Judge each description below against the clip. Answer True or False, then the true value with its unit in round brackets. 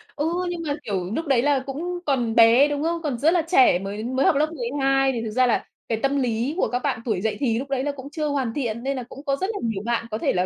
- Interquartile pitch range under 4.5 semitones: True (4.0 semitones)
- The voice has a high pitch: True (265 Hz)